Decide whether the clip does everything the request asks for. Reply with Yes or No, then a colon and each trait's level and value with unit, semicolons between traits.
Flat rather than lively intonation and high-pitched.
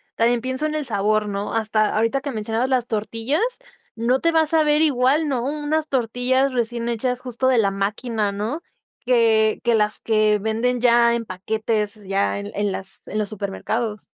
No: average, 3.3 semitones; high, 230 Hz